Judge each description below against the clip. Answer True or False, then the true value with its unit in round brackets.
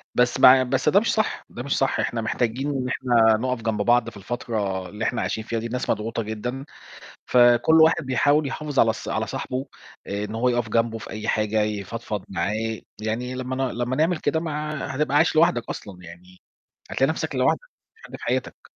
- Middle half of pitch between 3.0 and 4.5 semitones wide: True (3.5 semitones)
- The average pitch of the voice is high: False (120 Hz)